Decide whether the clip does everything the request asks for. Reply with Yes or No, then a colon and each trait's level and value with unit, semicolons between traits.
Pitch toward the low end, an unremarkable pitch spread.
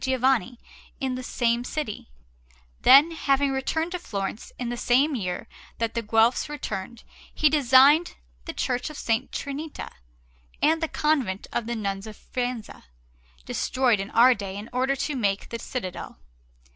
No: very high, 250 Hz; average, 4.0 semitones